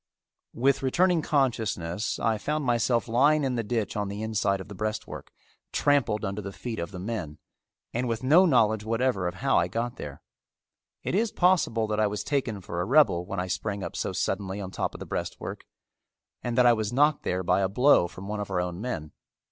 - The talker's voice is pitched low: Yes, low, 110 Hz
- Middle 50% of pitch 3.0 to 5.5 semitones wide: Yes, average, 4.6 semitones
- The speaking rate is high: Yes, fast, 210 wpm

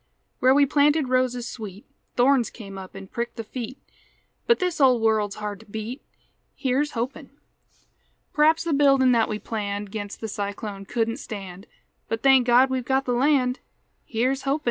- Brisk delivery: No, average, 165 wpm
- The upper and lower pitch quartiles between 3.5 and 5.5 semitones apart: Yes, average, 4.1 semitones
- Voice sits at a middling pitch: No, high, 245 Hz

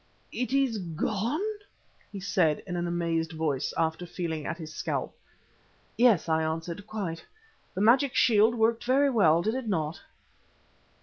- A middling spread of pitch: No, wide, 5.8 semitones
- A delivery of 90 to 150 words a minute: Yes, average, 145 wpm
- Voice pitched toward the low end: No, medium, 180 Hz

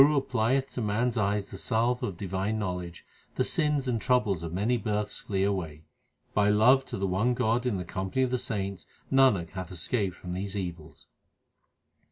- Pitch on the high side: No, low, 105 Hz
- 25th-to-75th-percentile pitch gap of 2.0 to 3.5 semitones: No, average, 4.8 semitones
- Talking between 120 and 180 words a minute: No, average, 200 wpm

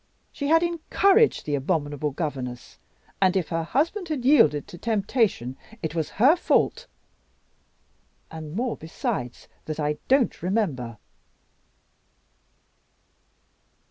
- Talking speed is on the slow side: Yes, slow, 110 wpm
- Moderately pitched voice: Yes, medium, 180 Hz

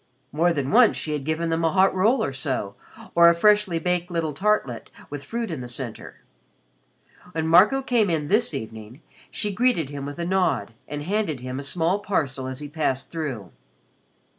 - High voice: No, medium, 165 Hz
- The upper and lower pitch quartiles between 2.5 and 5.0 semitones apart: No, wide, 5.6 semitones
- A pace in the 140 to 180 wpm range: No, average, 190 wpm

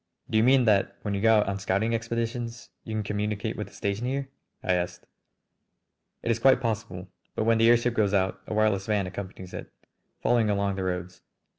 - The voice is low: Yes, low, 105 Hz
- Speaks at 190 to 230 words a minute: Yes, average, 200 wpm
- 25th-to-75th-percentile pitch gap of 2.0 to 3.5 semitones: Yes, average, 2.8 semitones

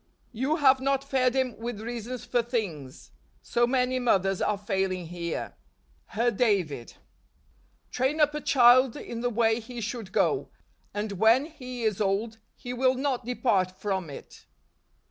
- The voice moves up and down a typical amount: Yes, average, 4.0 semitones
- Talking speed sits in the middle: Yes, average, 155 wpm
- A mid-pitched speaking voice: No, high, 235 Hz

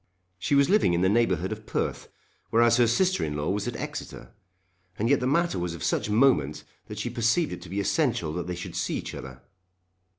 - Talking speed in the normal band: No, fast, 220 wpm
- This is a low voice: Yes, low, 110 Hz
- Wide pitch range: Yes, wide, 6.2 semitones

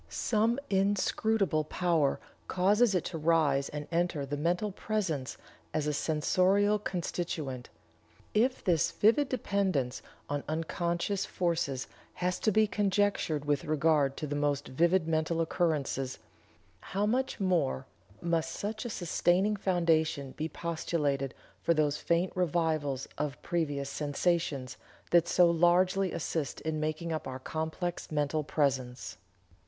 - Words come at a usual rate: No, slow, 125 wpm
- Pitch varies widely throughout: No, average, 4.1 semitones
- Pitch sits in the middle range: Yes, medium, 165 Hz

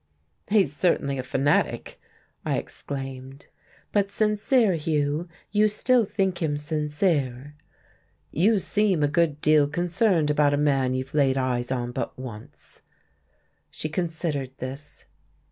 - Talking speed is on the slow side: Yes, slow, 125 wpm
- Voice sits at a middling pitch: Yes, medium, 150 Hz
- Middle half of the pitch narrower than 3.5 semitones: No, average, 4.9 semitones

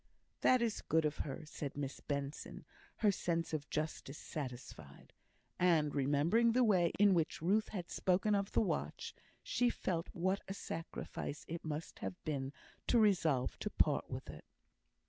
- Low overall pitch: No, medium, 165 Hz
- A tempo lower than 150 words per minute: No, average, 160 wpm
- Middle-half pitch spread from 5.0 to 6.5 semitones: Yes, average, 5.3 semitones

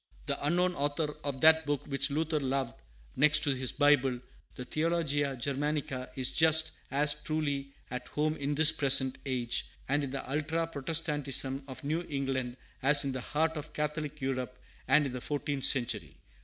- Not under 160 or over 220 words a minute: Yes, average, 170 wpm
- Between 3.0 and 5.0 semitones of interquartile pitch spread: No, narrow, 2.4 semitones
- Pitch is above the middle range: No, medium, 145 Hz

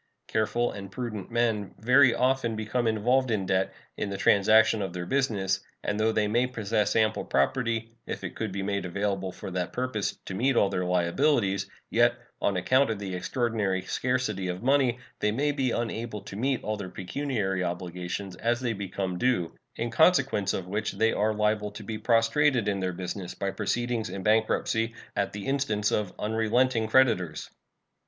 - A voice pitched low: Yes, low, 110 Hz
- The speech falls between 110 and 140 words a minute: No, average, 175 wpm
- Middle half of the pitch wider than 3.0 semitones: Yes, average, 3.7 semitones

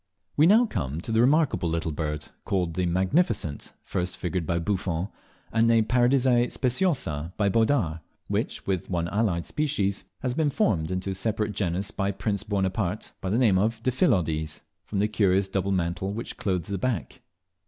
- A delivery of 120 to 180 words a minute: Yes, average, 170 wpm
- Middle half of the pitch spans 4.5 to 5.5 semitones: Yes, average, 4.9 semitones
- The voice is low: Yes, low, 100 Hz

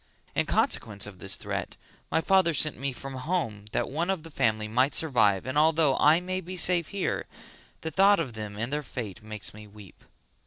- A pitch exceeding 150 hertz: No, low, 135 Hz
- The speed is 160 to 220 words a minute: Yes, average, 200 wpm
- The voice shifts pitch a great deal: Yes, wide, 7.4 semitones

